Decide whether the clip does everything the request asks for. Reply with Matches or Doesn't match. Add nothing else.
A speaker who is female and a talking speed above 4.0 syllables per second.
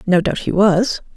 Matches